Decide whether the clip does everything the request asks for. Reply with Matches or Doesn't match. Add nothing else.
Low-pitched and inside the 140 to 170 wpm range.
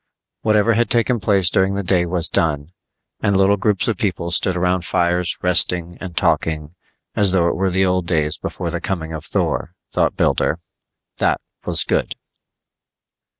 Matches